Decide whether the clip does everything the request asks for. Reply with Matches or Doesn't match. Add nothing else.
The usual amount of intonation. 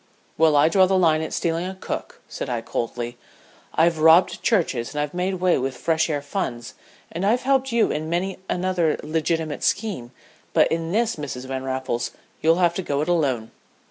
Matches